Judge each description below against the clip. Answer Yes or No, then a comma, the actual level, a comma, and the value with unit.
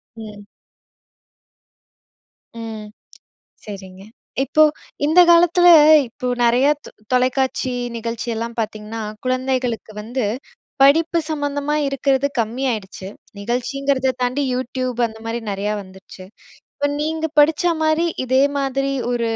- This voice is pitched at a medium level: No, very high, 255 Hz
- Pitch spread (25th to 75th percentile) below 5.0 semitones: Yes, average, 3.9 semitones